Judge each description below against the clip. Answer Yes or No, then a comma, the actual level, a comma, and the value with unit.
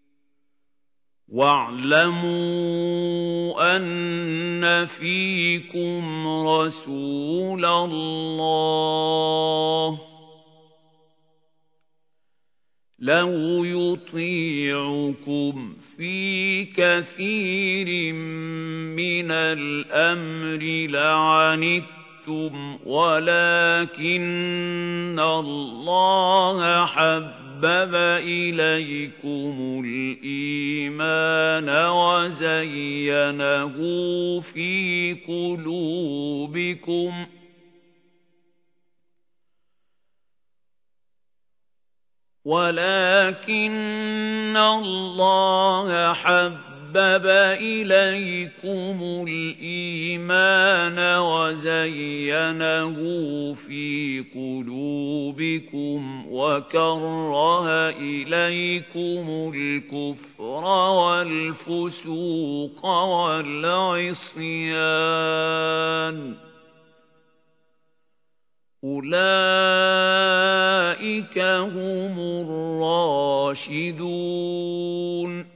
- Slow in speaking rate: Yes, slow, 30 wpm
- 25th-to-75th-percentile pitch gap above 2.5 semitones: No, narrow, 1.8 semitones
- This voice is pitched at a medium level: Yes, medium, 165 Hz